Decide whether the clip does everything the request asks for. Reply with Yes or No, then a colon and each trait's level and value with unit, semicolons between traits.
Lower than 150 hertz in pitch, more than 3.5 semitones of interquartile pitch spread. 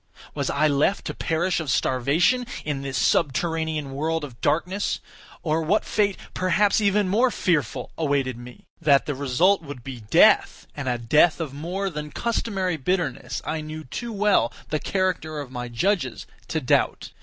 No: medium, 155 Hz; average, 5.2 semitones